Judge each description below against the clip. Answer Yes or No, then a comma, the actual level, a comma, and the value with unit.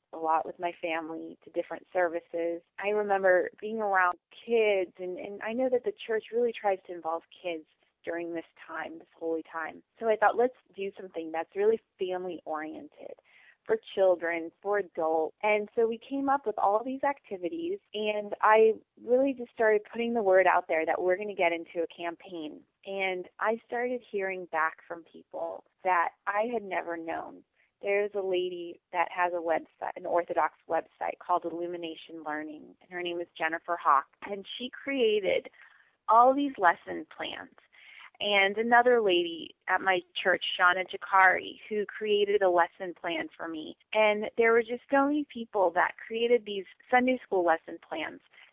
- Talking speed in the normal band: Yes, average, 170 wpm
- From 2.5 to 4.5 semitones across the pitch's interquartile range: No, average, 5.1 semitones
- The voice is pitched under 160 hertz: No, high, 195 Hz